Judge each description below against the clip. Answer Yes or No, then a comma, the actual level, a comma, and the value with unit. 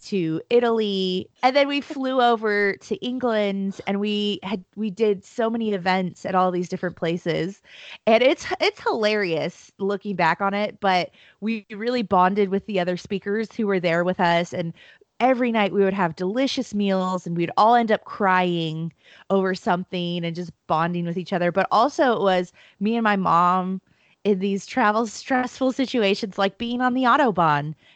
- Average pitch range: Yes, average, 3.9 semitones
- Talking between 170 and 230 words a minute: Yes, average, 180 wpm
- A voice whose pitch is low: No, high, 200 Hz